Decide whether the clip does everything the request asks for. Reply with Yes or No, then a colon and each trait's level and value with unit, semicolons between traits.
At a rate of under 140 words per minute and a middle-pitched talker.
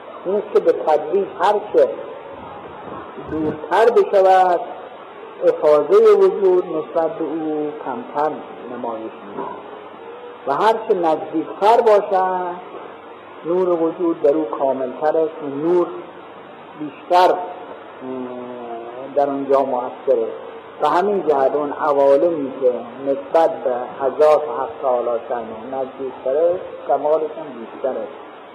Yes: average, 110 wpm; medium, 160 Hz